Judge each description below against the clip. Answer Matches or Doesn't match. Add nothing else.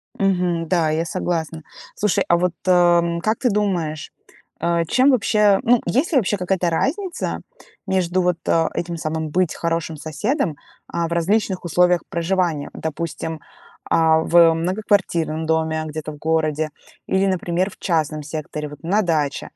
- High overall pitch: Doesn't match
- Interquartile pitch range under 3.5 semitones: Matches